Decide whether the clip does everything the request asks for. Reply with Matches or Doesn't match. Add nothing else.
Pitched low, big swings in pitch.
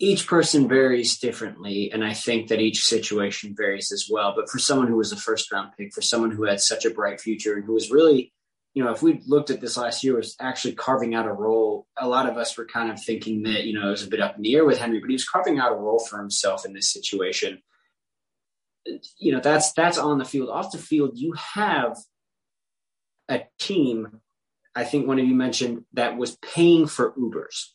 Doesn't match